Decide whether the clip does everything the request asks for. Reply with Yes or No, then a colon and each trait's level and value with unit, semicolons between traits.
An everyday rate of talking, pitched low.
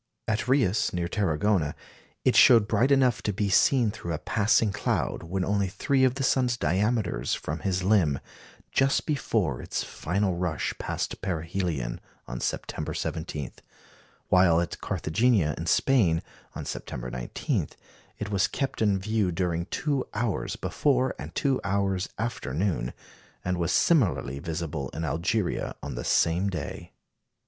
Yes: average, 145 wpm; very low, 95 Hz